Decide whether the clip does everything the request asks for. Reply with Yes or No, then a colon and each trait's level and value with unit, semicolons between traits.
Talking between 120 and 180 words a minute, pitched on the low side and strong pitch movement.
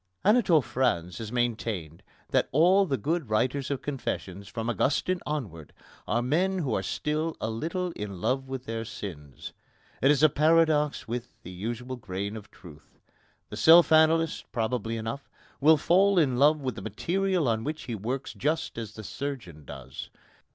Yes: average, 165 wpm; low, 130 Hz; wide, 6.0 semitones